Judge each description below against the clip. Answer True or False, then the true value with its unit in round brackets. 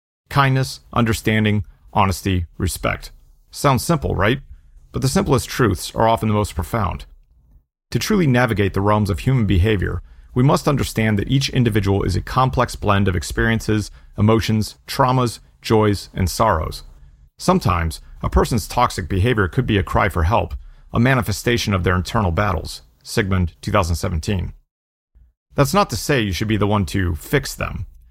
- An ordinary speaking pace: True (155 wpm)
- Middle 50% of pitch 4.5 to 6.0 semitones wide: True (5.4 semitones)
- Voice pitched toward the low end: True (100 Hz)